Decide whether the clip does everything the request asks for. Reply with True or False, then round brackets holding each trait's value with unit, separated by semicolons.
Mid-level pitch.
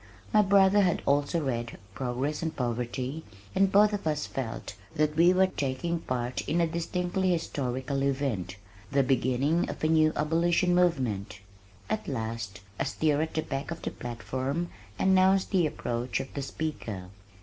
True (145 Hz)